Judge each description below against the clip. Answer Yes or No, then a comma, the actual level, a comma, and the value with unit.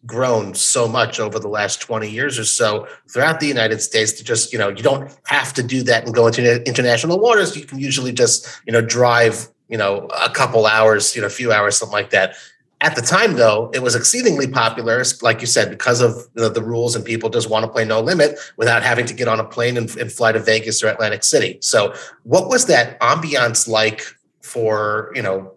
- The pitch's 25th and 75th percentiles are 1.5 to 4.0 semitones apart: Yes, average, 2.8 semitones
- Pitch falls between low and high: No, low, 120 Hz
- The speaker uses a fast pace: Yes, fast, 230 wpm